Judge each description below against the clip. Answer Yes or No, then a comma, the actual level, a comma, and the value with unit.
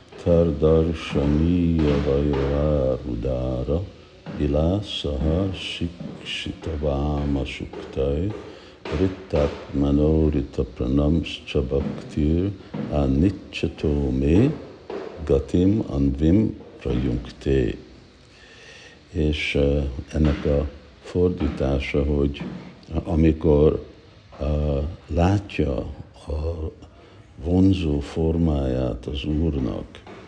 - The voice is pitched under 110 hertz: Yes, very low, 75 Hz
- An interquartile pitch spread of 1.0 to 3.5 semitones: Yes, average, 2.9 semitones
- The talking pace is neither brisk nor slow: No, slow, 60 wpm